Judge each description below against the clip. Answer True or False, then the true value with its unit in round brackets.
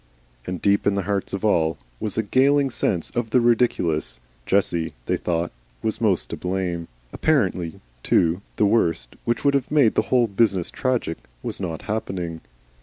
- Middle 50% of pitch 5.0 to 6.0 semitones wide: True (5.5 semitones)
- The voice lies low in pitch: True (100 Hz)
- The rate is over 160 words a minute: True (170 wpm)